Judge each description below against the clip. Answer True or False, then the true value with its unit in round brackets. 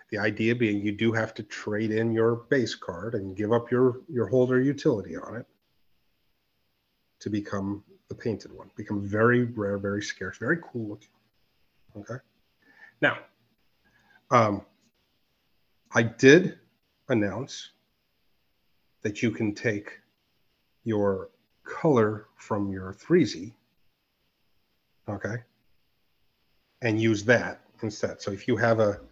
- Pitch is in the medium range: False (110 Hz)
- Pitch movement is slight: True (2.2 semitones)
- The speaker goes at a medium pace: False (120 wpm)